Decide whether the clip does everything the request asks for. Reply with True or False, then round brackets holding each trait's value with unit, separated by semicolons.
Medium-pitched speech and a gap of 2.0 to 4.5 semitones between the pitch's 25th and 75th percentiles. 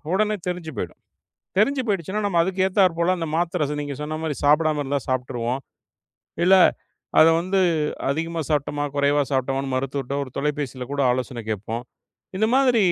False (150 Hz; 4.9 semitones)